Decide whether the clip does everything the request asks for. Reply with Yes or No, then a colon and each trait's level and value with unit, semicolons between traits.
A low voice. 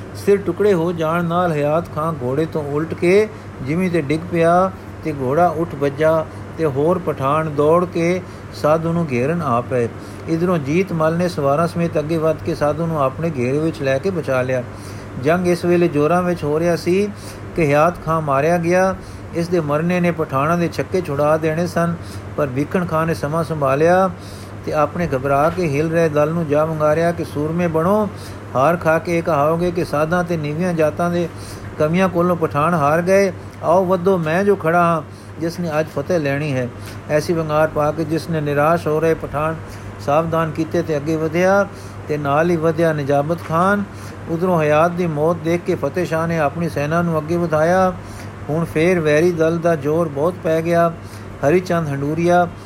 No: medium, 160 Hz